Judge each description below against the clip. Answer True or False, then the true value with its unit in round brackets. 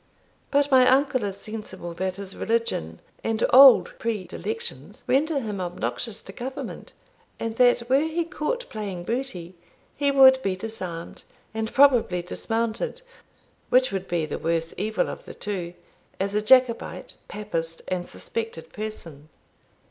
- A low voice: False (220 Hz)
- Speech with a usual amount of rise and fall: False (6.0 semitones)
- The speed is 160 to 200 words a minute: False (140 wpm)